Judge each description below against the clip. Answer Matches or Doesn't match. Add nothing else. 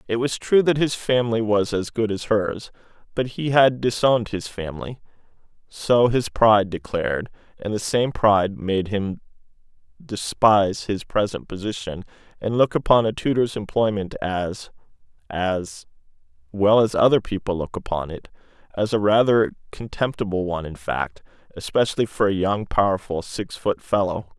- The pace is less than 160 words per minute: Matches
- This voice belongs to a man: Matches